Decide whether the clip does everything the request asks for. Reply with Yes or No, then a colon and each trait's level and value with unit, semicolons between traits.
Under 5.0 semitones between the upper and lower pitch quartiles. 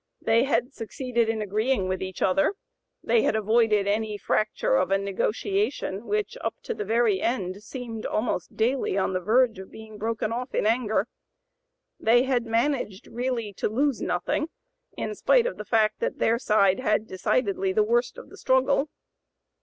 Yes: average, 3.8 semitones